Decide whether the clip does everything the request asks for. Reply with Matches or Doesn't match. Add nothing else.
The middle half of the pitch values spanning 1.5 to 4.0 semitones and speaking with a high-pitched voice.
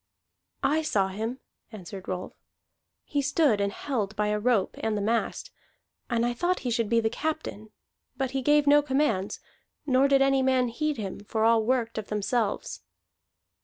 Doesn't match